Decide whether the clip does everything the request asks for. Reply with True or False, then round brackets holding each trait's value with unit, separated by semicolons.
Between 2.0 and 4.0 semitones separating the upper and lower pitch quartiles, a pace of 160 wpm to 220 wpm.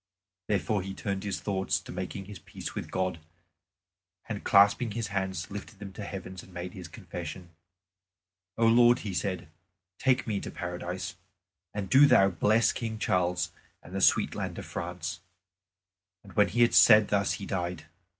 True (2.7 semitones; 170 wpm)